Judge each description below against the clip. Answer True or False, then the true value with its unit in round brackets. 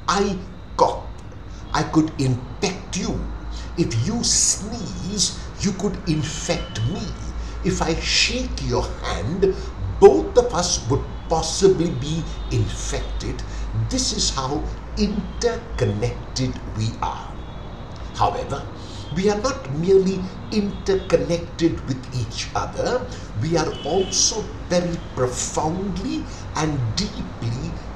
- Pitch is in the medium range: True (150 Hz)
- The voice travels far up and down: True (8.5 semitones)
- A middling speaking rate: False (100 wpm)